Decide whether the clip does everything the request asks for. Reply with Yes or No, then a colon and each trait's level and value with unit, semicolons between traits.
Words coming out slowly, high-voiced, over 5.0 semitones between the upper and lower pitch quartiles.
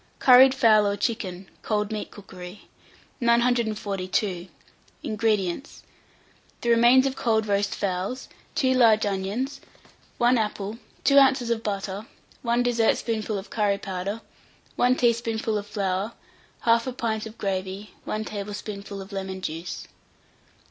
No: slow, 125 wpm; high, 215 Hz; average, 3.1 semitones